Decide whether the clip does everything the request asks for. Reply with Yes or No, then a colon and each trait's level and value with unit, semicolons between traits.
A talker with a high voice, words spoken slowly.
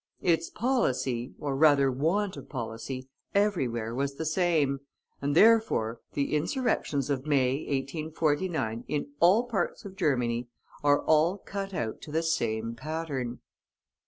No: medium, 145 Hz; slow, 130 wpm